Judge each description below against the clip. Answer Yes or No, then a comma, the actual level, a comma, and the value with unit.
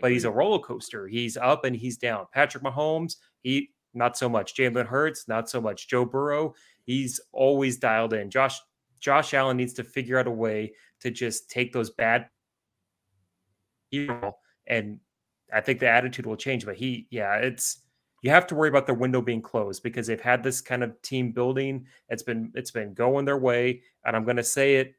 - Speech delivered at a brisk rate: No, average, 195 wpm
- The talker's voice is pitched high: No, low, 125 Hz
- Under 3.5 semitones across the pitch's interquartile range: Yes, average, 2.7 semitones